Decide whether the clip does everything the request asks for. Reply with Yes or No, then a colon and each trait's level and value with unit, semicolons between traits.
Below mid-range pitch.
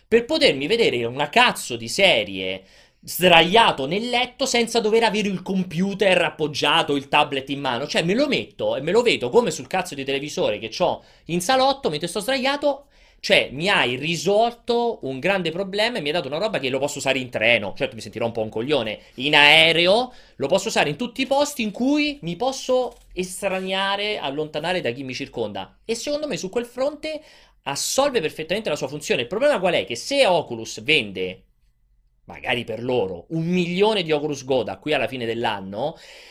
No: medium, 185 Hz